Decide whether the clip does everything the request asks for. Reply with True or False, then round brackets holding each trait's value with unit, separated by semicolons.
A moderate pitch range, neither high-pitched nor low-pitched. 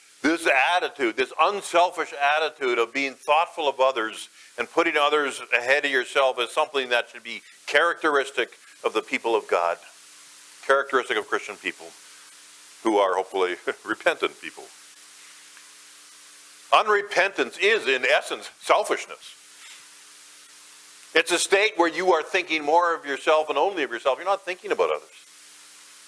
False (7.1 semitones; 155 Hz)